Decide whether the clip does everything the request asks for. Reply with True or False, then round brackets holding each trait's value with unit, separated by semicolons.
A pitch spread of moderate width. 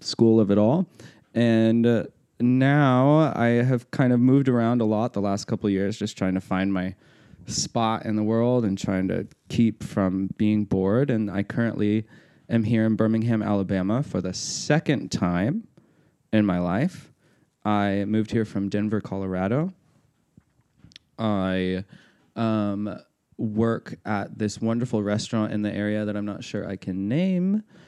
True (3.3 semitones)